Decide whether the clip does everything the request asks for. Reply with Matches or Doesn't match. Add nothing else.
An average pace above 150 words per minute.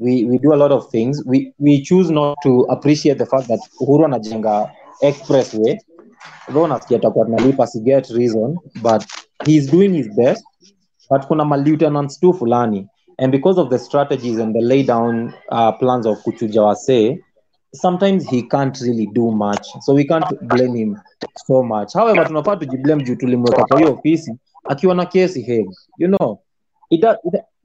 Matches